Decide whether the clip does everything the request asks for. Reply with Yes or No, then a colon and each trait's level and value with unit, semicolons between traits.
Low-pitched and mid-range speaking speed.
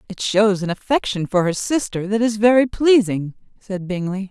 No: high, 205 Hz; average, 180 wpm